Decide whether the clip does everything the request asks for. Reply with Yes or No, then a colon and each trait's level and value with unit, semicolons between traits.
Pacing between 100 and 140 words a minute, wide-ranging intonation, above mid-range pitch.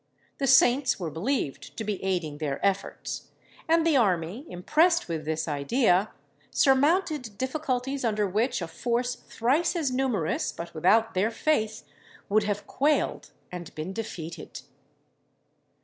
Yes: slow, 135 wpm; wide, 7.1 semitones; high, 220 Hz